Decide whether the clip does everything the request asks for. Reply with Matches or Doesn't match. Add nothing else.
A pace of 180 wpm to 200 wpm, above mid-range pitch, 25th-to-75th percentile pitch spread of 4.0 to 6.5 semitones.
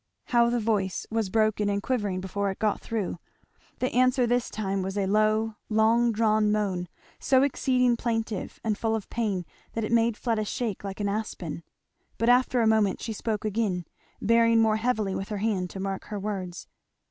Doesn't match